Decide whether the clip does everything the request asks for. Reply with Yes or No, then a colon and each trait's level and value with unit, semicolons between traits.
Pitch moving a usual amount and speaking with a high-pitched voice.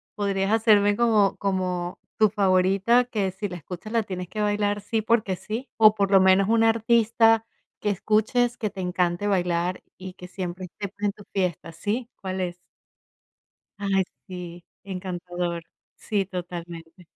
Yes: average, 3.0 semitones; high, 195 Hz